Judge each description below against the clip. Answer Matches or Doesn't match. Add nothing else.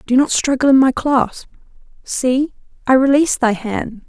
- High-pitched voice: Matches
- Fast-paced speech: Doesn't match